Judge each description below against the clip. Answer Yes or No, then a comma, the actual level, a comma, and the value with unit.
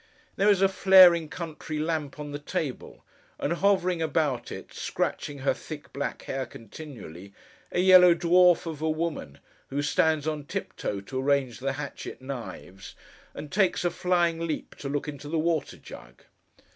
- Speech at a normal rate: Yes, average, 160 wpm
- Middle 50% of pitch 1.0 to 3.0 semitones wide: No, average, 3.6 semitones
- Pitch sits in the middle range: Yes, medium, 155 Hz